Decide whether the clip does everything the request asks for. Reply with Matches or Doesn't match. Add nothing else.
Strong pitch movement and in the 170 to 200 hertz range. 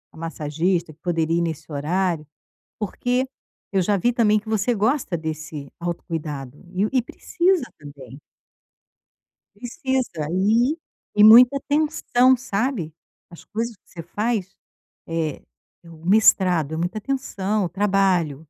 Matches